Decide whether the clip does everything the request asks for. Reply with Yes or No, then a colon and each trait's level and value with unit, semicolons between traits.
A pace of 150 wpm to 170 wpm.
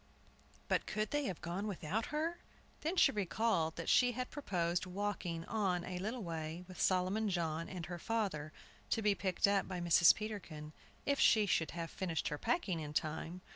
No: average, 180 wpm